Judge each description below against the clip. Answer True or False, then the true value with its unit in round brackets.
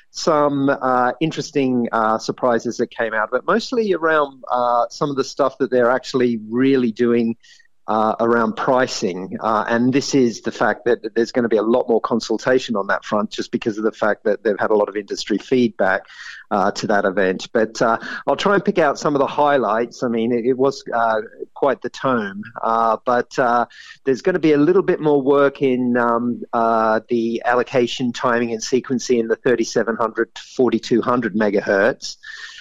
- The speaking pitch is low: True (125 Hz)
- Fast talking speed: False (195 wpm)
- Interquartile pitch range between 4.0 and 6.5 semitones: False (3.4 semitones)